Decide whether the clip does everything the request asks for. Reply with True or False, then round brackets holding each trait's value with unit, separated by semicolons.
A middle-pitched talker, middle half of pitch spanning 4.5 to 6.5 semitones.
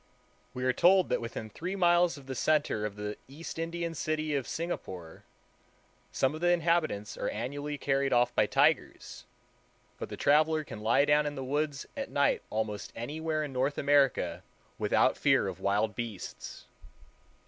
True (145 Hz; 4.8 semitones)